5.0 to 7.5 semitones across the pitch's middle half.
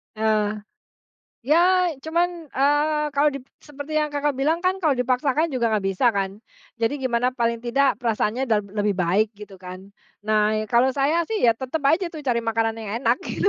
Yes: average, 5.3 semitones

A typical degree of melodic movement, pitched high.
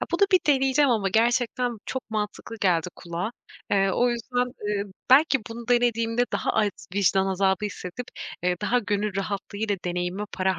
Yes: average, 4.0 semitones; high, 210 Hz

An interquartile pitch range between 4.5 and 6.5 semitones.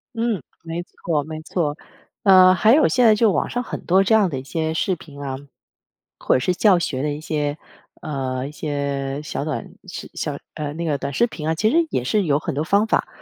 Yes: average, 5.2 semitones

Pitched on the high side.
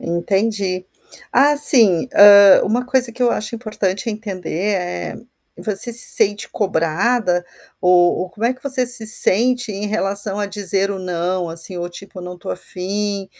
Yes: high, 200 Hz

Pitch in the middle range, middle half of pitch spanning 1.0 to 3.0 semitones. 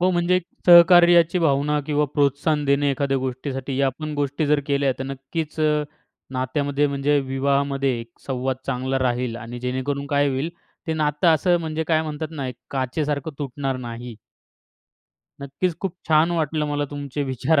Yes: medium, 145 Hz; average, 2.7 semitones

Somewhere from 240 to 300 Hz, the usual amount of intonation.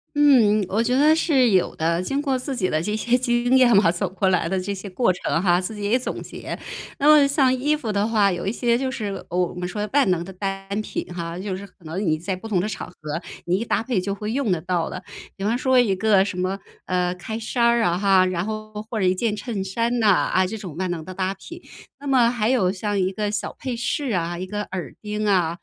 No: high, 205 Hz; average, 4.4 semitones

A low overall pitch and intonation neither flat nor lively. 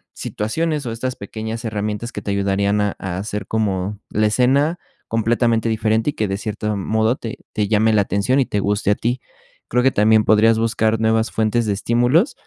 No: low, 110 Hz; narrow, 2.1 semitones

